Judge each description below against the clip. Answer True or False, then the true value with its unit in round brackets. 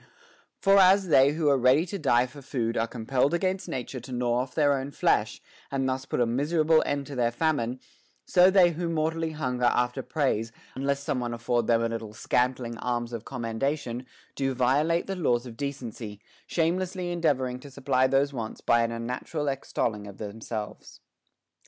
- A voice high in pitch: False (130 Hz)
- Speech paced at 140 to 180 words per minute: False (190 wpm)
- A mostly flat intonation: False (4.4 semitones)